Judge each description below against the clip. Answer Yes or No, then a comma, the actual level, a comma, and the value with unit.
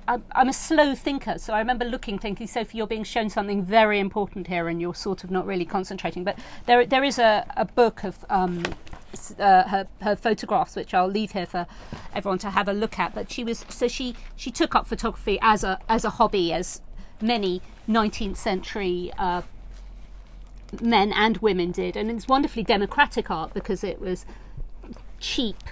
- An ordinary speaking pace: Yes, average, 185 wpm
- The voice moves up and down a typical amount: Yes, average, 3.4 semitones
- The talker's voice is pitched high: Yes, high, 210 Hz